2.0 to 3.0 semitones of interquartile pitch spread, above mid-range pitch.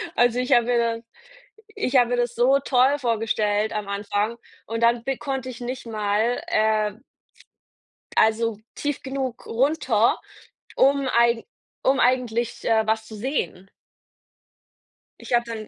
Yes: average, 2.7 semitones; high, 235 Hz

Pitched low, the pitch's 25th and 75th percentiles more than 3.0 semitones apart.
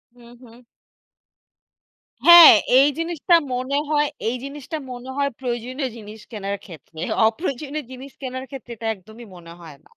No: very high, 255 Hz; average, 3.9 semitones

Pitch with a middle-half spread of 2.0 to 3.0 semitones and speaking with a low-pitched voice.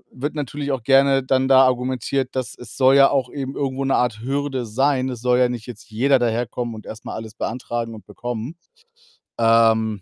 Yes: average, 2.7 semitones; low, 125 Hz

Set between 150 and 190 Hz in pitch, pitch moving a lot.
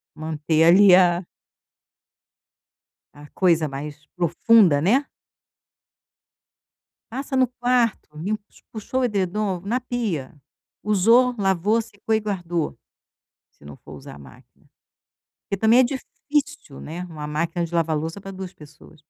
Yes: medium, 185 Hz; wide, 6.0 semitones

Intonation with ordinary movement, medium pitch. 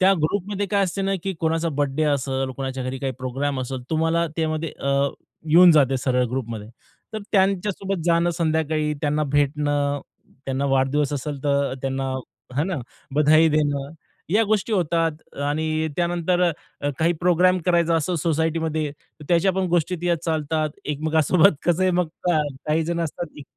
Yes: average, 3.4 semitones; medium, 155 Hz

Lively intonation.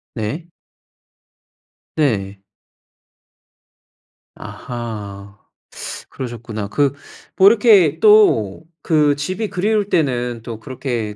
Yes: wide, 8.0 semitones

